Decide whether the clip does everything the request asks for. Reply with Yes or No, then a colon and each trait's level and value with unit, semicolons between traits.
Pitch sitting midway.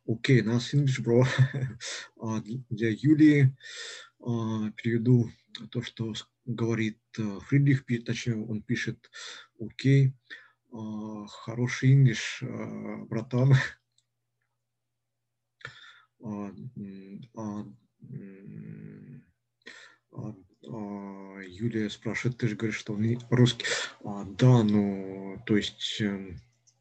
No: low, 115 Hz